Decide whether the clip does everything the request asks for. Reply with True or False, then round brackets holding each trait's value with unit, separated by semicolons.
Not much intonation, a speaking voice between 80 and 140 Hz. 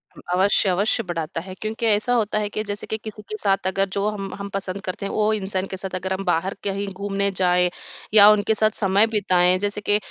False (2.0 semitones; 200 Hz)